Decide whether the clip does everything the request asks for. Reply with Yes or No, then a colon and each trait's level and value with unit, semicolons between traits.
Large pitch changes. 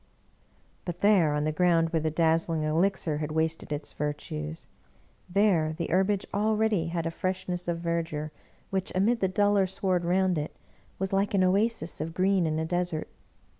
No: average, 3.2 semitones